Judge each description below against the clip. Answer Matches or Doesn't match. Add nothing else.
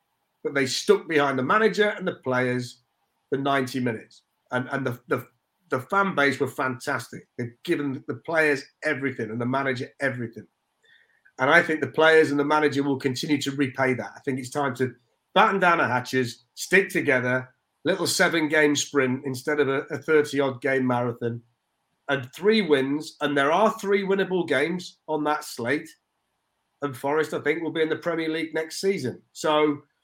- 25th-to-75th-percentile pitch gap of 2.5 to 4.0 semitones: Matches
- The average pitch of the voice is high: Doesn't match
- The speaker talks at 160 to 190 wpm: Matches